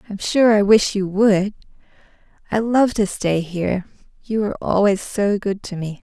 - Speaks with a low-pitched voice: No, high, 200 Hz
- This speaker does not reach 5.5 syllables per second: Yes, 4.7 syllables/s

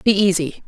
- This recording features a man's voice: No, female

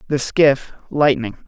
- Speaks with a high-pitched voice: No, low, 135 Hz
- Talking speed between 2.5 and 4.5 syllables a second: Yes, 3.9 syllables/s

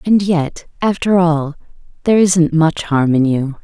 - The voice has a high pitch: No, medium, 165 Hz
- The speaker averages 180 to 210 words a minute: No, average, 165 wpm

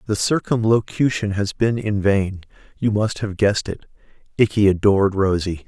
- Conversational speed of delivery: No, slow, 125 wpm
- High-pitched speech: No, low, 105 Hz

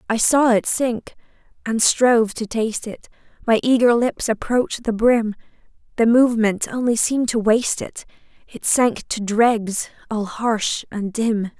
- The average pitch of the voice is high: Yes, high, 225 Hz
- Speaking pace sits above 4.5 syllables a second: No, 4.4 syllables/s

